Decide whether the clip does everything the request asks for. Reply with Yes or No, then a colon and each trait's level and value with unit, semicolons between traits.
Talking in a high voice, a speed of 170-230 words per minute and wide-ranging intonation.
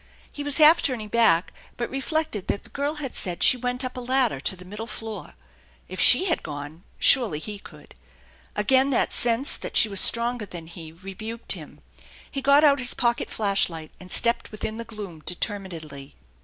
Yes: high, 225 Hz; average, 190 wpm; wide, 5.9 semitones